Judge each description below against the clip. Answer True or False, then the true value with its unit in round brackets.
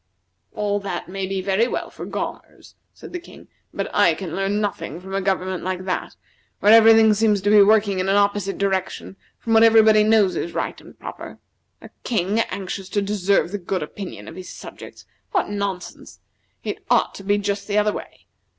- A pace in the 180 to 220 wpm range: True (195 wpm)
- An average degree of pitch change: False (1.8 semitones)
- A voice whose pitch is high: True (200 Hz)